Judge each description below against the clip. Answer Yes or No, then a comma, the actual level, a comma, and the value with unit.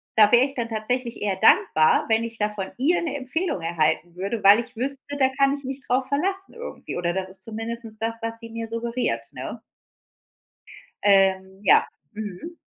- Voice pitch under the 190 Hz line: No, high, 230 Hz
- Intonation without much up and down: No, average, 4.9 semitones